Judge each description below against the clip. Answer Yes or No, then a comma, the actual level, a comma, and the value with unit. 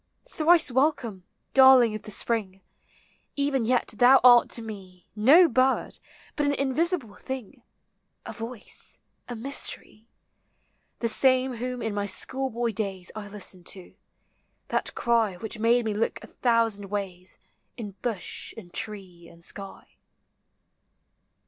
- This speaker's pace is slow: Yes, slow, 130 wpm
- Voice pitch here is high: Yes, high, 230 Hz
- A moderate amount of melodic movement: Yes, average, 4.1 semitones